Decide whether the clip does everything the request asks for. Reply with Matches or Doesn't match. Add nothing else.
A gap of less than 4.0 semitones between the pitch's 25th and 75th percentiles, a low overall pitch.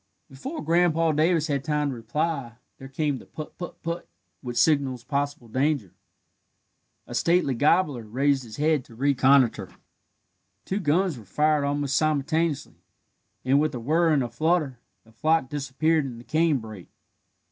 Doesn't match